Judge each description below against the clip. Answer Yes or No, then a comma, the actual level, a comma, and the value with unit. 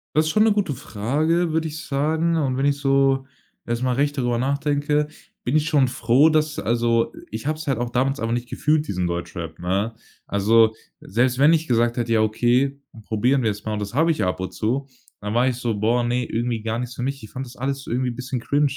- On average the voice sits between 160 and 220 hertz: No, low, 125 Hz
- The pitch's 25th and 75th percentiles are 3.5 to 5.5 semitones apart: Yes, average, 3.8 semitones